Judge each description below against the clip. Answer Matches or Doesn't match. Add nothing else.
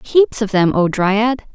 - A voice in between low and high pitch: Doesn't match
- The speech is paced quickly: Doesn't match